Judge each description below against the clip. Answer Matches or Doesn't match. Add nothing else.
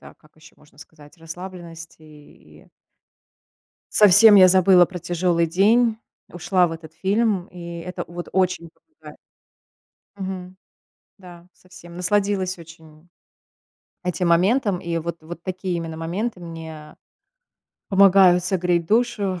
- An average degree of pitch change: Doesn't match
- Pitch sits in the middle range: Matches